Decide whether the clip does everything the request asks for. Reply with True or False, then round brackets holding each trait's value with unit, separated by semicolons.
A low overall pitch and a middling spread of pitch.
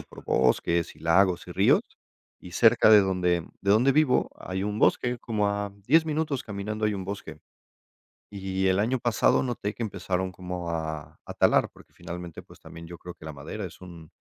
True (95 Hz; 3.8 semitones)